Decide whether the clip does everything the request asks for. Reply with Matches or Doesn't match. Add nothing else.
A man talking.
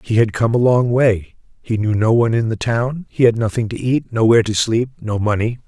Matches